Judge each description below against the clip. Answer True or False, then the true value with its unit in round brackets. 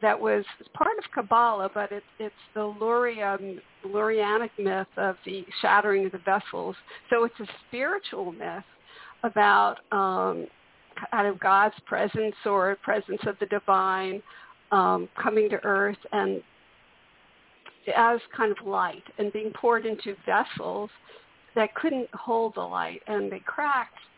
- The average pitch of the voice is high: True (210 Hz)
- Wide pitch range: False (2.7 semitones)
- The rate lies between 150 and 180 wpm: False (140 wpm)